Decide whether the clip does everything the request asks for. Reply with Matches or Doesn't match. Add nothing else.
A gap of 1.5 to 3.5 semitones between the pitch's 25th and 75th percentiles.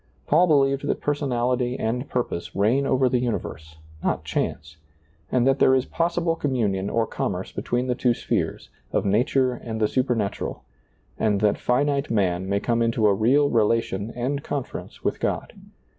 Doesn't match